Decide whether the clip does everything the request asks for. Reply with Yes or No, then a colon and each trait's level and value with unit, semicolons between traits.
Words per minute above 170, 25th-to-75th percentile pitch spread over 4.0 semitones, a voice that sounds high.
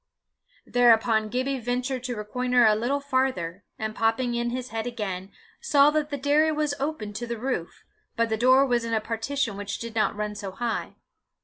No: average, 190 wpm; average, 3.2 semitones; high, 240 Hz